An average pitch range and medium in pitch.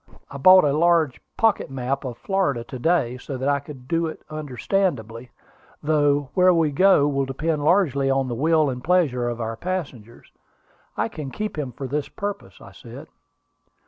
Yes: average, 4.4 semitones; medium, 145 Hz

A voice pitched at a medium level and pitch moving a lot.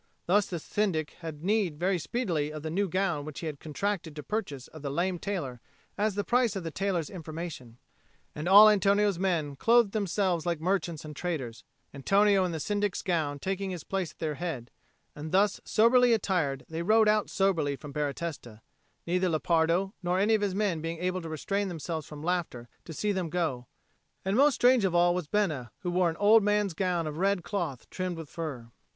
No: medium, 175 Hz; average, 4.2 semitones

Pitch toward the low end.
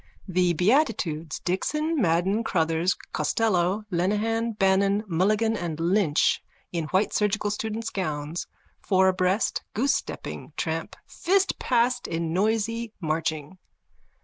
No: high, 195 Hz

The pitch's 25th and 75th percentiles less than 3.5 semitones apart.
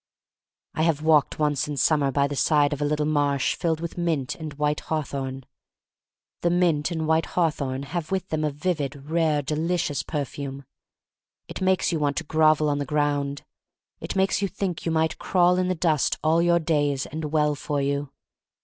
Yes: narrow, 2.4 semitones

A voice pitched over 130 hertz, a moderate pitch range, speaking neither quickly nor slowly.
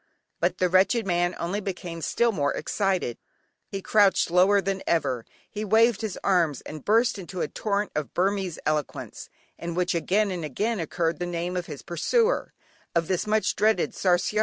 Yes: medium, 185 Hz; average, 3.4 semitones; average, 175 wpm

